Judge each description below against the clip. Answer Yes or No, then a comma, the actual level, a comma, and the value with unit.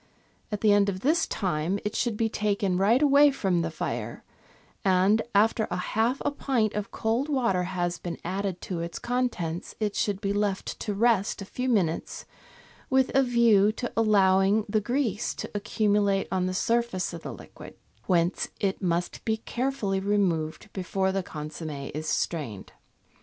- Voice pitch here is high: Yes, high, 200 Hz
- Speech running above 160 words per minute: Yes, average, 170 wpm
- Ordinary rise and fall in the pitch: Yes, average, 3.7 semitones